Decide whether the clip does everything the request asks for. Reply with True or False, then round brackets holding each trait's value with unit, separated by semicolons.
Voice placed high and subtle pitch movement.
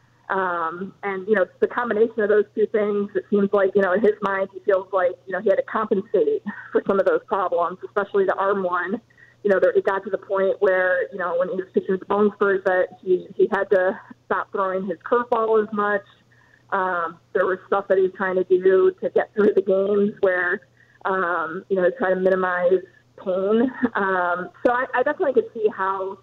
True (195 Hz; 2.2 semitones)